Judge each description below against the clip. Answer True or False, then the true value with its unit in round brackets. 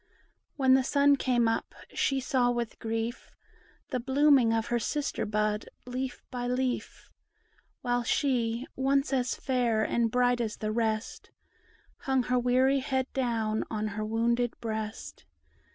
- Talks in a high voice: True (245 Hz)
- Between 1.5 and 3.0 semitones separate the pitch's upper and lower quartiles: True (2.6 semitones)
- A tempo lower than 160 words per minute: True (140 wpm)